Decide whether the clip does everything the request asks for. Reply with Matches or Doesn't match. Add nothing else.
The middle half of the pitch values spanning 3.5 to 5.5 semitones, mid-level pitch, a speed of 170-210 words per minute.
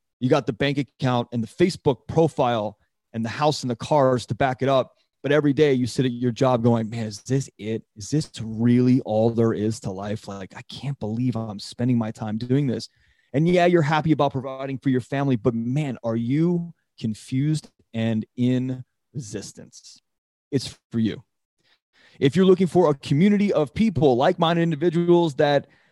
Doesn't match